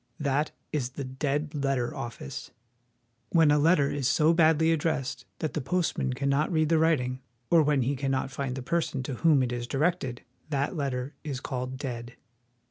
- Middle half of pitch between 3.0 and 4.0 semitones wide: Yes, average, 3.4 semitones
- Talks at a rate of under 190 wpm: Yes, average, 175 wpm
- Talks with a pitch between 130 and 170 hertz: Yes, medium, 140 Hz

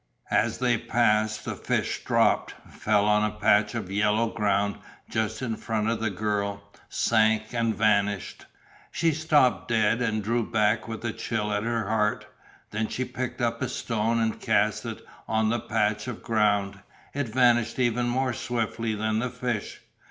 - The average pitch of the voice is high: No, low, 110 Hz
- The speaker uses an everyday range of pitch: No, narrow, 1.9 semitones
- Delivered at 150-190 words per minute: Yes, average, 165 wpm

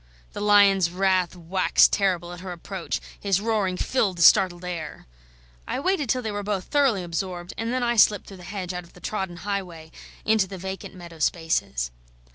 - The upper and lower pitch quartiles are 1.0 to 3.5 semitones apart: Yes, average, 2.8 semitones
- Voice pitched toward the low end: No, high, 190 Hz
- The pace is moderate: Yes, average, 190 wpm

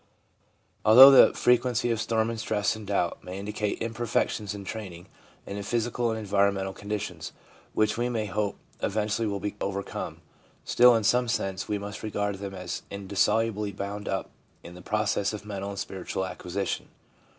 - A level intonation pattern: Yes, narrow, 2.1 semitones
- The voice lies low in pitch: Yes, low, 105 Hz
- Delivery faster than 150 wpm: Yes, average, 170 wpm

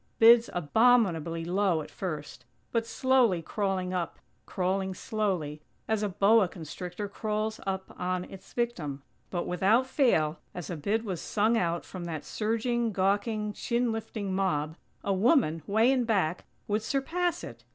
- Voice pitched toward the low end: No, high, 195 Hz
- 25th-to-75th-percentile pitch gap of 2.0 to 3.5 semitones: No, average, 4.2 semitones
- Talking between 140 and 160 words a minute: Yes, average, 150 wpm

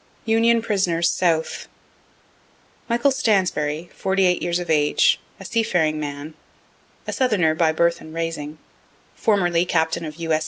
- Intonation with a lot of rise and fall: No, average, 3.7 semitones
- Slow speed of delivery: Yes, slow, 130 wpm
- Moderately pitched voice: Yes, medium, 170 Hz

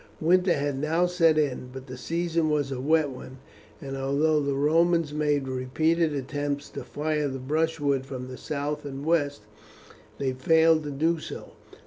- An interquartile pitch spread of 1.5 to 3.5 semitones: Yes, average, 3.0 semitones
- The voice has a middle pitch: Yes, medium, 145 Hz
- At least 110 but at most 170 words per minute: Yes, average, 165 wpm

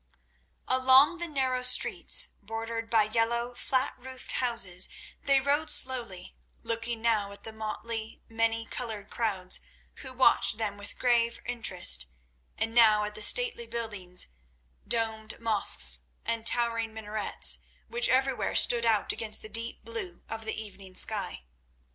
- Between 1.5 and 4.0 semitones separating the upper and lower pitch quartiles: Yes, narrow, 2.4 semitones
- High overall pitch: Yes, high, 230 Hz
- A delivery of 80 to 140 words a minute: Yes, slow, 135 wpm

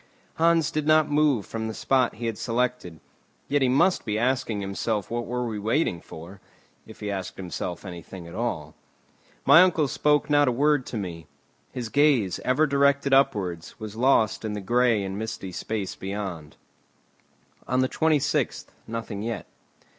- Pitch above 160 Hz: No, low, 115 Hz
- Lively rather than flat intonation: Yes, wide, 5.8 semitones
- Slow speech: No, average, 165 wpm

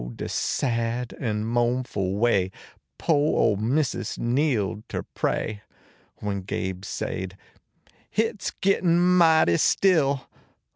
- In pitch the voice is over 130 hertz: No, low, 120 Hz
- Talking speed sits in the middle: No, slow, 110 wpm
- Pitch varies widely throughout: Yes, wide, 7.1 semitones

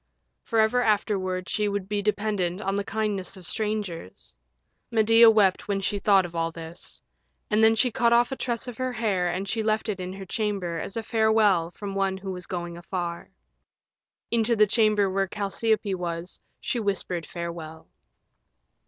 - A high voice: Yes, high, 200 Hz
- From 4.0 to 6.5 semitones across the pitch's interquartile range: No, average, 3.2 semitones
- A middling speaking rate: Yes, average, 170 wpm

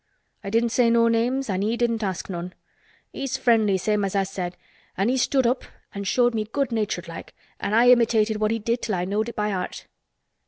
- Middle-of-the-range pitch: No, high, 220 Hz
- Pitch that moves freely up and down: No, average, 3.2 semitones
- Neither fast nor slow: No, fast, 220 wpm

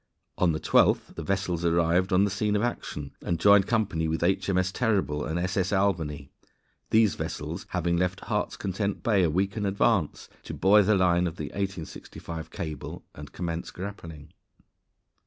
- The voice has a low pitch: Yes, very low, 90 Hz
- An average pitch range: Yes, average, 3.3 semitones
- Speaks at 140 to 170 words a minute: Yes, average, 165 wpm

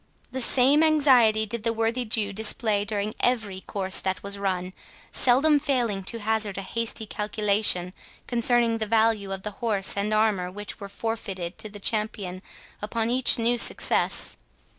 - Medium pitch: No, high, 215 Hz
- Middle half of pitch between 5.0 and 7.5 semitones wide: No, average, 2.7 semitones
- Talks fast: No, average, 160 wpm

